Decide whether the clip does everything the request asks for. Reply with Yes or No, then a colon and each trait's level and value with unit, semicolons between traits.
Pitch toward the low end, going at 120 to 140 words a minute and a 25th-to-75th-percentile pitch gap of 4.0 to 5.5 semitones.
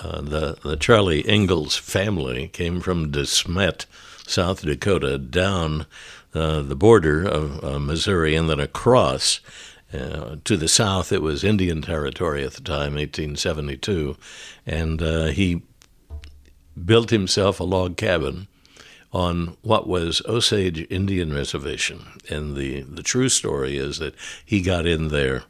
Yes: very low, 80 Hz; slow, 135 wpm; average, 4.5 semitones